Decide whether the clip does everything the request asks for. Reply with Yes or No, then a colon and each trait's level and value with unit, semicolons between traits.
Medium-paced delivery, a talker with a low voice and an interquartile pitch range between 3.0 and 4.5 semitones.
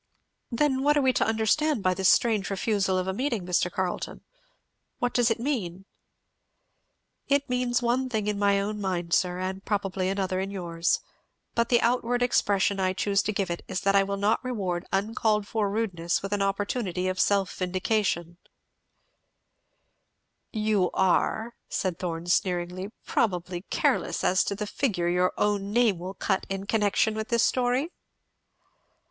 No: average, 160 wpm; high, 200 Hz; average, 3.5 semitones